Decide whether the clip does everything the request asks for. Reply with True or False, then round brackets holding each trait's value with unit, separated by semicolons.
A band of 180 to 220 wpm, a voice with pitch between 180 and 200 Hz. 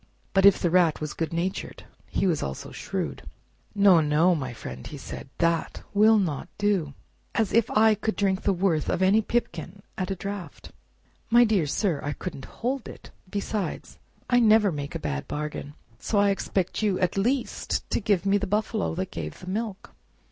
True (185 wpm; 190 Hz)